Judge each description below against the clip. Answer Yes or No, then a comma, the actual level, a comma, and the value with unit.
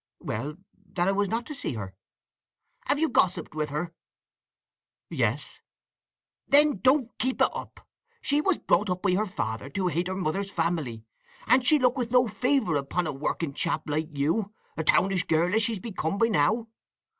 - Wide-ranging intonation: Yes, wide, 6.8 semitones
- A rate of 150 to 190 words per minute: Yes, average, 170 wpm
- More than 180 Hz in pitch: Yes, high, 190 Hz